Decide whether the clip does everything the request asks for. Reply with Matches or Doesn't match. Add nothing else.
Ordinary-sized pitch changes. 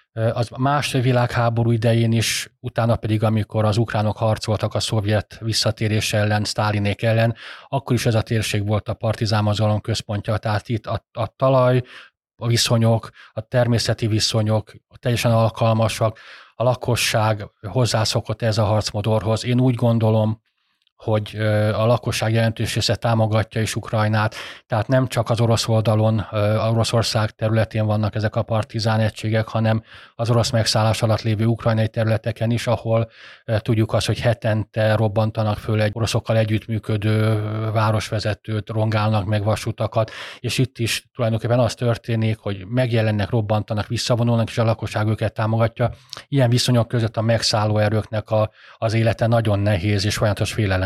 Doesn't match